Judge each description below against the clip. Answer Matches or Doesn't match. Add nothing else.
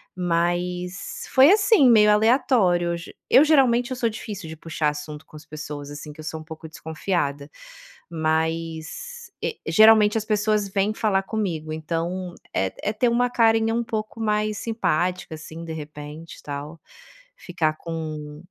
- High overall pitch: Doesn't match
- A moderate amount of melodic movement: Doesn't match